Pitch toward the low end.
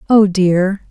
No: high, 190 Hz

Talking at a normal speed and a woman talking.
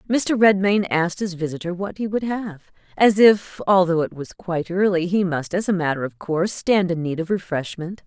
No: fast, 210 wpm; female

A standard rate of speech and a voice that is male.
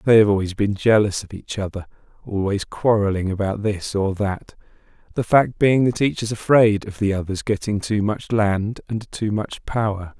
Yes: average, 190 wpm; male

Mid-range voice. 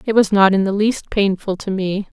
No: high, 200 Hz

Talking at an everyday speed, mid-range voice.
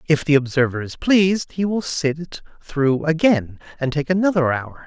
Yes: average, 185 wpm; medium, 155 Hz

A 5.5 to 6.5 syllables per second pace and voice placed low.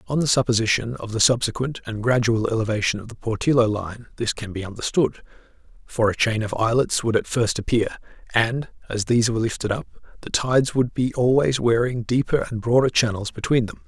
Yes: 5.8 syllables/s; low, 115 Hz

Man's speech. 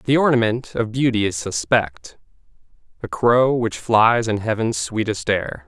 Yes: male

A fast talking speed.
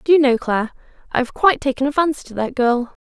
Yes: fast, 235 wpm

